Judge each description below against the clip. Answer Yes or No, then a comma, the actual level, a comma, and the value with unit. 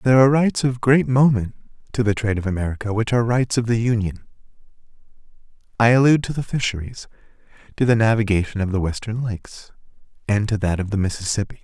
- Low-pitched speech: Yes, low, 110 Hz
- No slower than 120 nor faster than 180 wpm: Yes, average, 175 wpm